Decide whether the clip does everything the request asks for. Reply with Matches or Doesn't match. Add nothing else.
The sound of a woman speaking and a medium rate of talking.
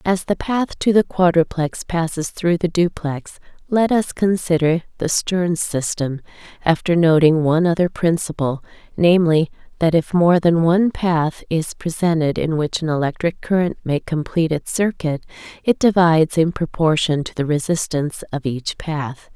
Matches